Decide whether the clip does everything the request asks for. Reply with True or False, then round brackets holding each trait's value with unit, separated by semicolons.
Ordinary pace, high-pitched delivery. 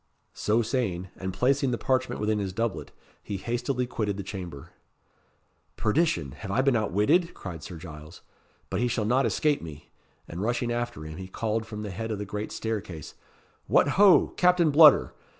False (175 wpm; 110 Hz)